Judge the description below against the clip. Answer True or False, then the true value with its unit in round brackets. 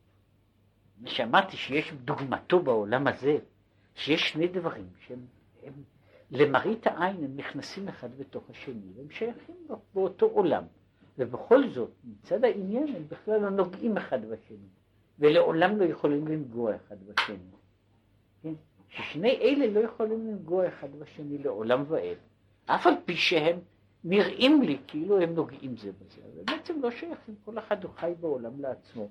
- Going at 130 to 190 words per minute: True (140 wpm)